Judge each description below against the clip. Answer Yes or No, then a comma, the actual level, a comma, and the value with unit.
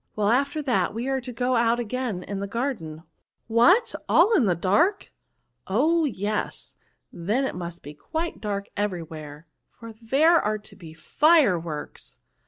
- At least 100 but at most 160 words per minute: No, average, 170 wpm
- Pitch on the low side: No, high, 225 Hz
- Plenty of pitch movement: Yes, wide, 6.9 semitones